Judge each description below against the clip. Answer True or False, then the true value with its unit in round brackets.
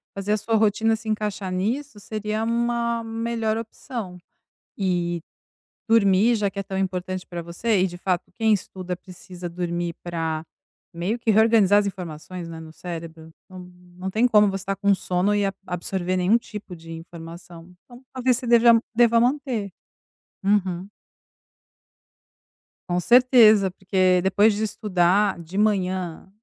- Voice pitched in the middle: False (195 Hz)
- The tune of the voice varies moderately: True (3.7 semitones)